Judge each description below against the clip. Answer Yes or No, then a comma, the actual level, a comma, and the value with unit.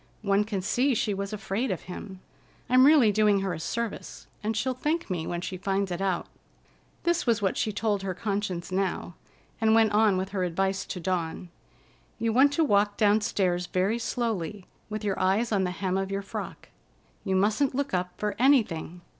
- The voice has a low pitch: No, high, 200 Hz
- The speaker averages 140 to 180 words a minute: No, average, 190 wpm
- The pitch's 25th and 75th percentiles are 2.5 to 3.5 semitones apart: Yes, average, 3.0 semitones